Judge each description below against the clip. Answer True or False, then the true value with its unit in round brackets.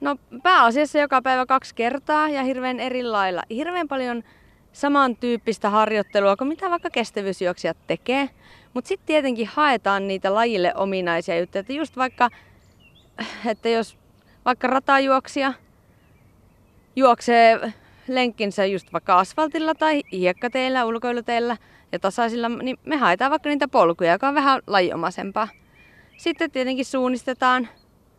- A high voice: True (245 Hz)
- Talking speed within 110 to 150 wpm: True (120 wpm)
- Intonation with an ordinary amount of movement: True (4.5 semitones)